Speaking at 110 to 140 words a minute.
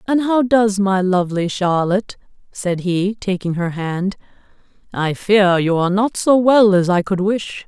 No: average, 170 wpm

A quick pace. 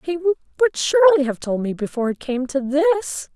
No: average, 195 wpm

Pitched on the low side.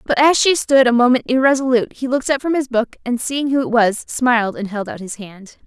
No: very high, 250 Hz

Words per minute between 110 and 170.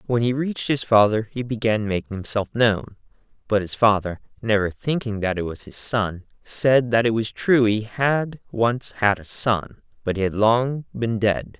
No: average, 190 wpm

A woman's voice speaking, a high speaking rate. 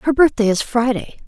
No: female; average, 190 wpm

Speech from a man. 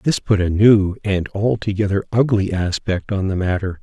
Yes: male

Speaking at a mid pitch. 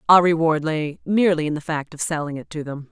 Yes: medium, 160 Hz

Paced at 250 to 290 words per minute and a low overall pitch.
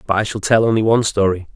Yes: fast, 270 wpm; low, 105 Hz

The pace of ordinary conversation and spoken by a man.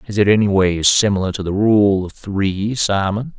Yes: average, 195 wpm; male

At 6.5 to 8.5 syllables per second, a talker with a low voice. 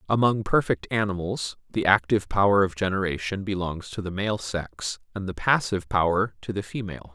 No: 5.5 syllables/s; low, 100 Hz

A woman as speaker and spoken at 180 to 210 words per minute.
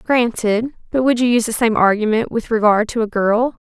Yes: female; average, 200 wpm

